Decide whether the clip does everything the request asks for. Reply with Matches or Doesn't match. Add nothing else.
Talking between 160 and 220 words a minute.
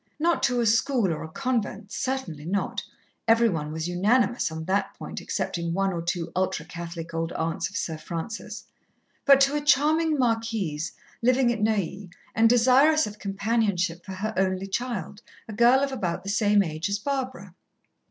Matches